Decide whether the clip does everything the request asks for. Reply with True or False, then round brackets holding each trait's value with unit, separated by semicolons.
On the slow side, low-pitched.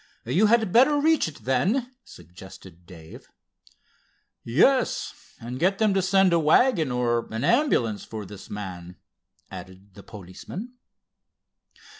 True (125 wpm; 125 Hz)